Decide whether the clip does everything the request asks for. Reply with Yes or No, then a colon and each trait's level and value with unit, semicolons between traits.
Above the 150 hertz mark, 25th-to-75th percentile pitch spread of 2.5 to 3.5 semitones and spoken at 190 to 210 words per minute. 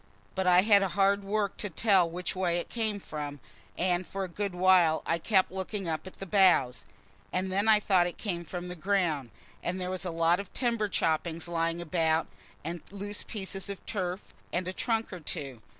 Yes: medium, 185 Hz; average, 2.8 semitones; average, 200 wpm